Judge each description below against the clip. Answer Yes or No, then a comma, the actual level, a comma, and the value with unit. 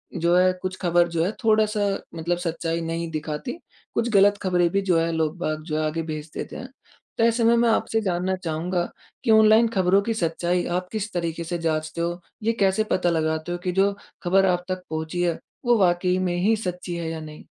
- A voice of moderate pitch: Yes, medium, 175 Hz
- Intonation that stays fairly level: No, average, 3.1 semitones